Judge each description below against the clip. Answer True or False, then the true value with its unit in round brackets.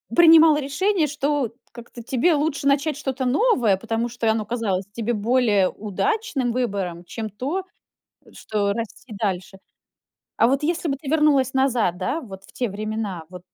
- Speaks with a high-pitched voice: True (245 Hz)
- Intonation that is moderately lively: False (5.7 semitones)